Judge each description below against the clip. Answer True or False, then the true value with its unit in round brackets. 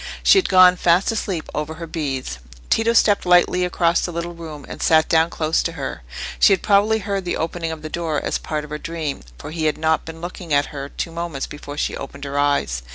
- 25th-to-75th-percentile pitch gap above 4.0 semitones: False (2.8 semitones)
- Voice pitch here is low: False (165 Hz)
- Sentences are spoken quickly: True (230 wpm)